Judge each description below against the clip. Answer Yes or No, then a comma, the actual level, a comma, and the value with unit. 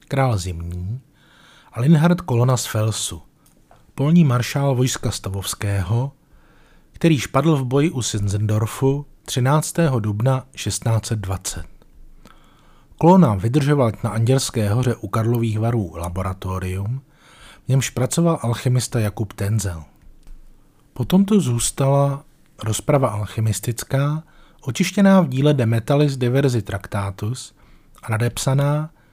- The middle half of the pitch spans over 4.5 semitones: Yes, average, 5.2 semitones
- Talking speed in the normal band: No, slow, 100 wpm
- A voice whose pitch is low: Yes, low, 125 Hz